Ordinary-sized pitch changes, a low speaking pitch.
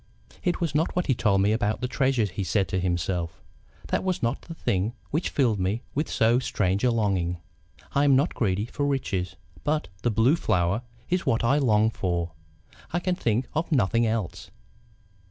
No: wide, 6.4 semitones; low, 115 Hz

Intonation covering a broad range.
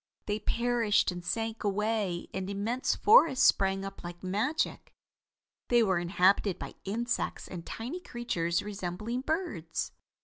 No: average, 4.4 semitones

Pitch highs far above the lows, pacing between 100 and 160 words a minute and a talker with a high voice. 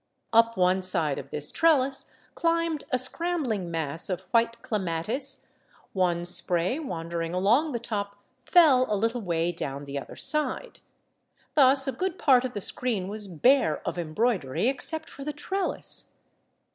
Yes: wide, 7.8 semitones; average, 150 wpm; high, 225 Hz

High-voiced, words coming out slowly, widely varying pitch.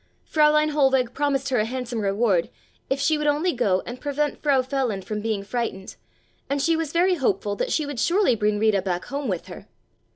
No: very high, 260 Hz; average, 200 wpm; wide, 5.7 semitones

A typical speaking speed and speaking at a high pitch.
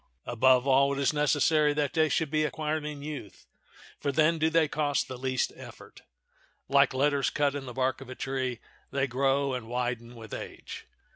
No: average, 190 wpm; medium, 140 Hz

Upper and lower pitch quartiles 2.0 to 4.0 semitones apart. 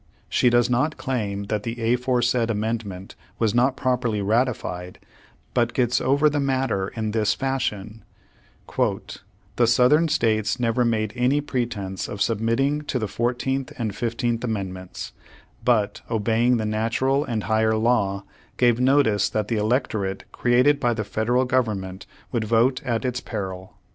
Yes: average, 2.8 semitones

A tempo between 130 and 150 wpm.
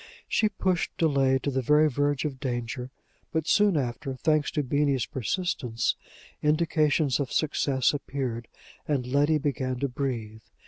Yes: average, 140 wpm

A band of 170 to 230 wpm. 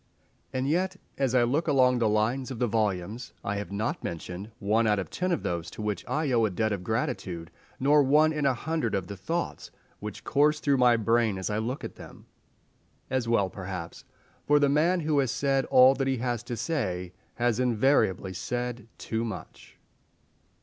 Yes: average, 195 wpm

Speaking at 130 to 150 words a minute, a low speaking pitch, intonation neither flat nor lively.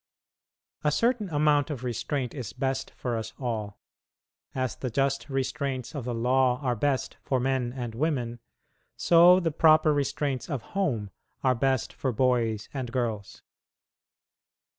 Yes: average, 140 wpm; low, 130 Hz; average, 3.2 semitones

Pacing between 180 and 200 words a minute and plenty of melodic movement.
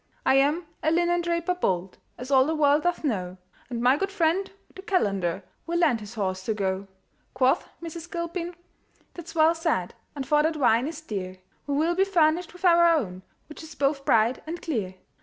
Yes: average, 190 wpm; wide, 7.1 semitones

